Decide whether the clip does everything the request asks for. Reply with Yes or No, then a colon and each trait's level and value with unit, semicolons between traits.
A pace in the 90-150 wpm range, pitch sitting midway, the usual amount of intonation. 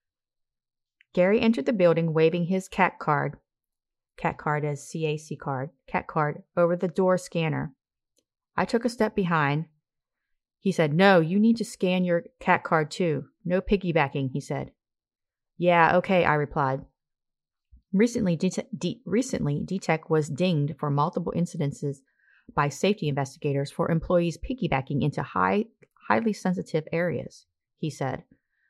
Yes: slow, 135 wpm; medium, 165 Hz; average, 4.0 semitones